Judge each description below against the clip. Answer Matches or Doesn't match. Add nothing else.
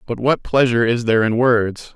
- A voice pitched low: Matches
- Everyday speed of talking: Doesn't match